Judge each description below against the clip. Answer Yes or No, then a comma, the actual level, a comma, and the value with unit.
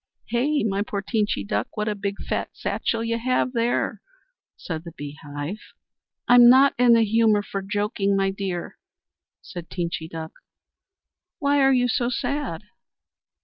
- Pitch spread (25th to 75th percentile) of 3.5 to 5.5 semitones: Yes, average, 4.8 semitones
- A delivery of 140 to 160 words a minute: Yes, average, 150 wpm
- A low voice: No, high, 210 Hz